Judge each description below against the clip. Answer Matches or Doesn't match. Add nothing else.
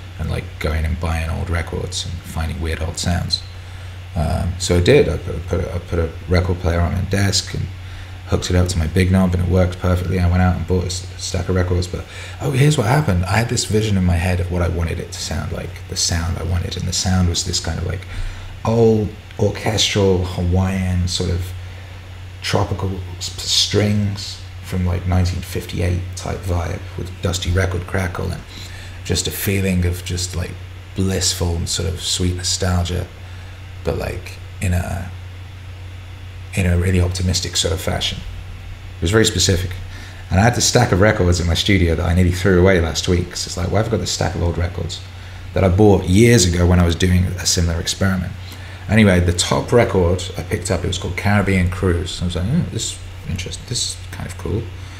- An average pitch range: Doesn't match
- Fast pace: Matches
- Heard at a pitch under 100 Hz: Matches